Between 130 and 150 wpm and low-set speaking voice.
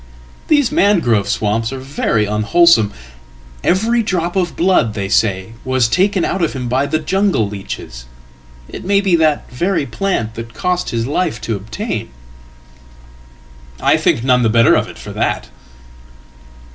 Yes: average, 140 wpm; low, 120 Hz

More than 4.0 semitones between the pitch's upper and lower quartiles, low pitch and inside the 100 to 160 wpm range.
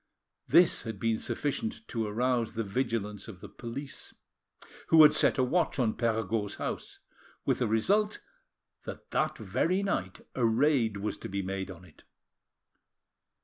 Yes: average, 5.0 semitones; low, 115 Hz; average, 150 wpm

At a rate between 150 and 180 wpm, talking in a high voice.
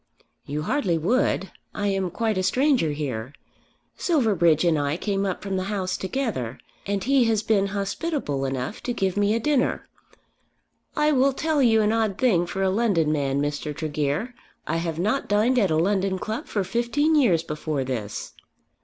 Yes: average, 175 wpm; high, 195 Hz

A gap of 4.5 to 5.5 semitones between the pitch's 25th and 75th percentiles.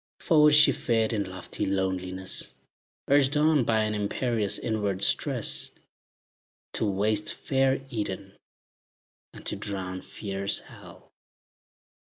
Yes: average, 5.0 semitones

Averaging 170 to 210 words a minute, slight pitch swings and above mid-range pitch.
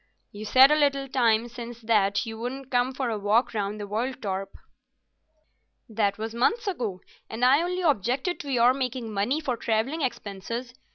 No: average, 175 wpm; average, 3.6 semitones; high, 240 Hz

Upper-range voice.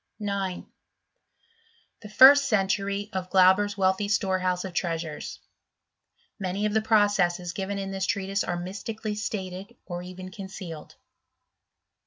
Yes: high, 195 Hz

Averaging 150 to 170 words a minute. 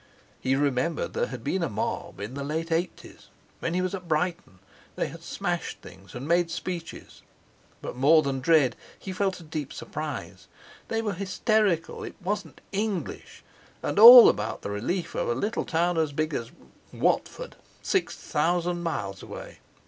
Yes: average, 160 wpm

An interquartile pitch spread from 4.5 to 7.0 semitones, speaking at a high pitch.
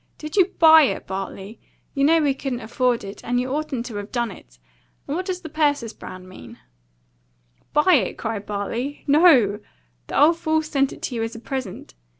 Yes: wide, 5.6 semitones; very high, 260 Hz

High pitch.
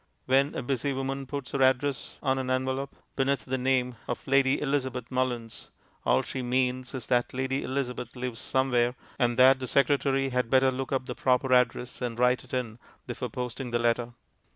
No: low, 130 Hz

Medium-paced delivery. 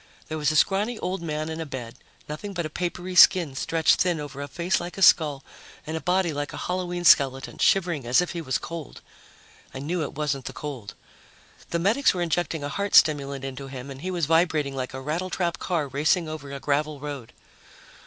No: fast, 210 wpm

